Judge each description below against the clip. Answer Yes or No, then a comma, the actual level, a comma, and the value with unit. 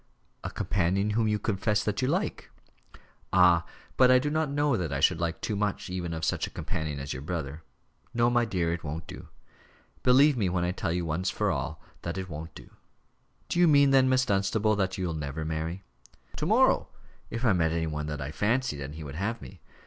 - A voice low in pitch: Yes, very low, 95 Hz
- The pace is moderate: No, fast, 215 wpm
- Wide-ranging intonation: Yes, wide, 6.0 semitones